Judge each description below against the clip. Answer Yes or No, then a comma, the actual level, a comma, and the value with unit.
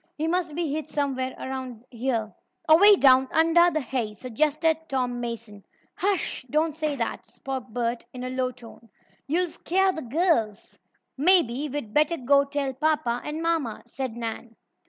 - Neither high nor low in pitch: No, very high, 270 Hz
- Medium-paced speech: Yes, average, 155 wpm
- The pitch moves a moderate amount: Yes, average, 4.6 semitones